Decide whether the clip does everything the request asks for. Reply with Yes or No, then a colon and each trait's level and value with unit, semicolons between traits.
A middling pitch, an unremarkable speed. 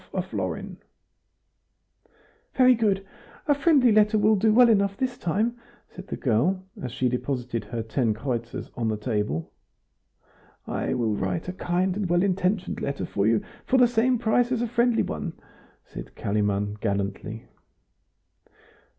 Yes: medium, 180 Hz; average, 150 wpm